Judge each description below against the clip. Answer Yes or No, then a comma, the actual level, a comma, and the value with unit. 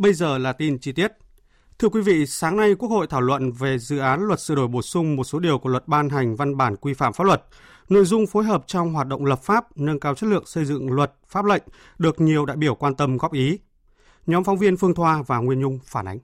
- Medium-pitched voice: Yes, medium, 150 Hz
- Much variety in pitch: Yes, wide, 5.7 semitones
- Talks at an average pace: No, fast, 265 wpm